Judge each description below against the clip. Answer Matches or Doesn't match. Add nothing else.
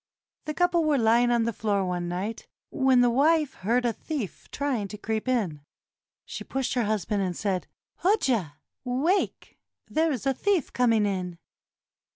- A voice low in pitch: Doesn't match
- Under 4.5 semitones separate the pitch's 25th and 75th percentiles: Doesn't match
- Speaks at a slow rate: Doesn't match